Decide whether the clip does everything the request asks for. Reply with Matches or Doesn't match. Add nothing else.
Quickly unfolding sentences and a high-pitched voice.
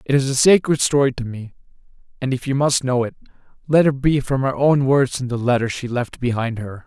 Doesn't match